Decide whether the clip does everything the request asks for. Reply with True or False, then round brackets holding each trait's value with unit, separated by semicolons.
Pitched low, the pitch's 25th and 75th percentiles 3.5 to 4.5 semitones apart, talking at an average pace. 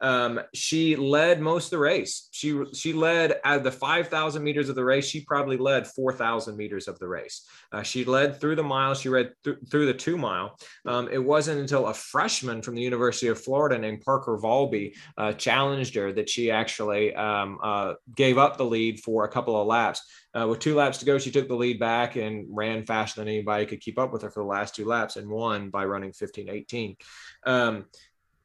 False (125 Hz; 4.2 semitones; 210 wpm)